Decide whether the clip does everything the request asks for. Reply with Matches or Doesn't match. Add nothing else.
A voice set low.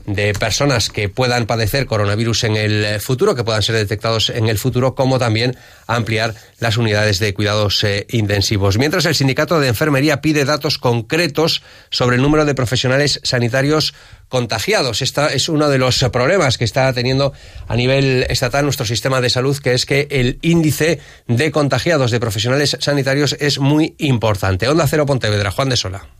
Matches